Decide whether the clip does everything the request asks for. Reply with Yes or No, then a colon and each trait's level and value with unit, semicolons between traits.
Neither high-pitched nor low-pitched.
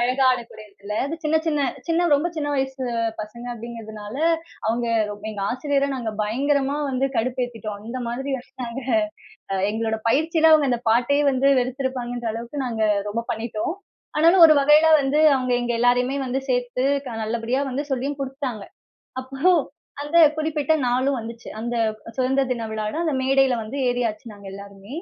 No: very high, 250 Hz